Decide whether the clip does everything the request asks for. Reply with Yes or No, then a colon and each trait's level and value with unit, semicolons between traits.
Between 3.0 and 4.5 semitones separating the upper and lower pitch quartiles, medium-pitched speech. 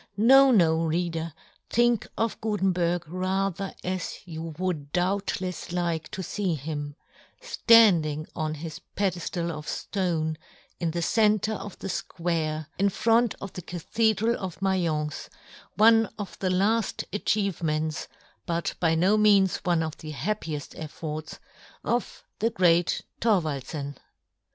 Yes: average, 4.0 semitones; medium, 180 Hz